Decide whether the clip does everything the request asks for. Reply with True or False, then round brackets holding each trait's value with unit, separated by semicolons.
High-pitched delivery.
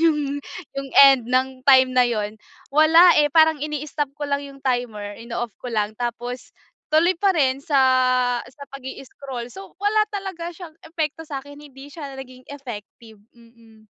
True (275 Hz)